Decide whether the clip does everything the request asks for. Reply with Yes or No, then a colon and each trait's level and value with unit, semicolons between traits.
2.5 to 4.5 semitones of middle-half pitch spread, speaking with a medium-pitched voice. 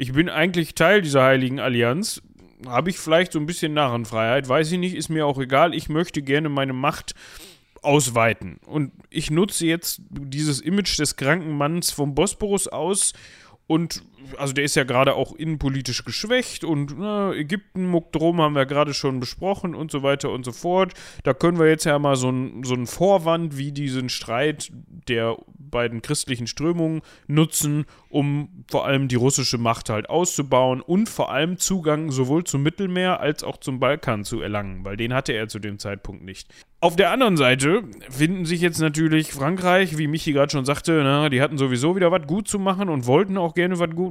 Yes: average, 4.1 semitones; medium, 150 Hz